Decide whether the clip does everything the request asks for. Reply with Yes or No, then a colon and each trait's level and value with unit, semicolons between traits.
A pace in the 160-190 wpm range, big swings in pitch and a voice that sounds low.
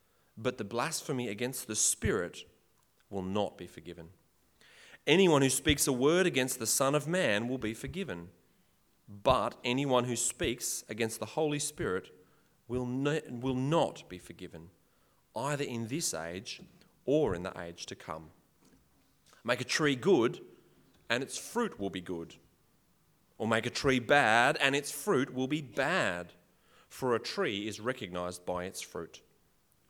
No: average, 150 wpm; wide, 7.0 semitones; low, 120 Hz